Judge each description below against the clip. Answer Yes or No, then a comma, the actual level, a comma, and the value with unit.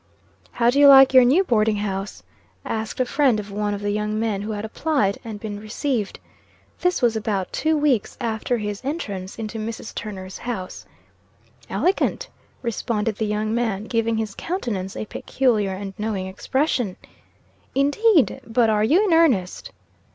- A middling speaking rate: Yes, average, 160 wpm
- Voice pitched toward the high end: Yes, high, 220 Hz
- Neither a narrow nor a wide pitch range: Yes, average, 3.9 semitones